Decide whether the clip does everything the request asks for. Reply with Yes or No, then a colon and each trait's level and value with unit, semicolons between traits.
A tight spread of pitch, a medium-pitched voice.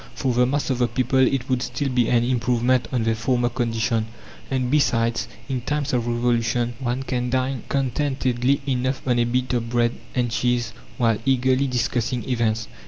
No: narrow, 1.6 semitones; low, 125 Hz